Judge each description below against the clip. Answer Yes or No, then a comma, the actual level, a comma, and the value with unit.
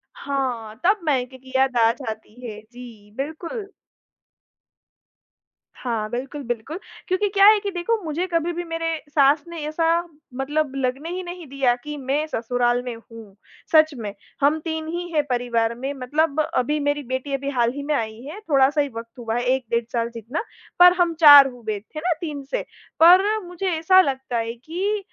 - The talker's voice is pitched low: No, very high, 280 Hz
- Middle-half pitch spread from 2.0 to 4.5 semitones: No, average, 5.3 semitones